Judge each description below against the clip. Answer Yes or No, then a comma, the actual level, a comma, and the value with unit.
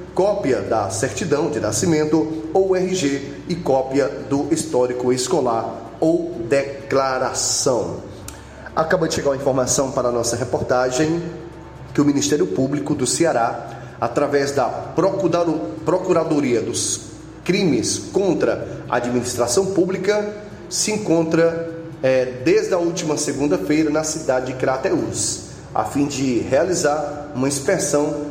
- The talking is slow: Yes, slow, 115 wpm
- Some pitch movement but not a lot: Yes, average, 4.2 semitones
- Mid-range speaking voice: Yes, medium, 145 Hz